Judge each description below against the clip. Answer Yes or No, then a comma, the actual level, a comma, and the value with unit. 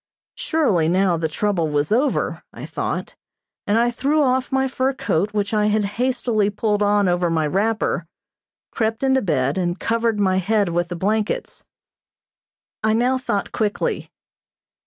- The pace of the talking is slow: No, average, 155 wpm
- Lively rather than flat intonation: No, average, 4.7 semitones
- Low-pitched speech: No, high, 210 Hz